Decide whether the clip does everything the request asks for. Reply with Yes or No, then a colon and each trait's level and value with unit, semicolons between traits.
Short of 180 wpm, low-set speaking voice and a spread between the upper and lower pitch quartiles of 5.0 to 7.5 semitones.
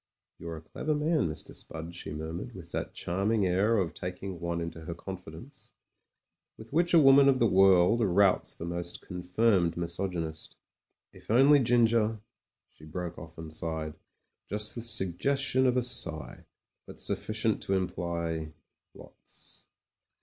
Yes: average, 155 wpm; very low, 95 Hz; wide, 5.5 semitones